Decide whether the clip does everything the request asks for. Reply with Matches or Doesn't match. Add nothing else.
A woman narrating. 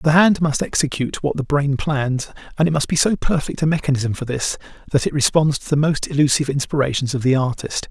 Doesn't match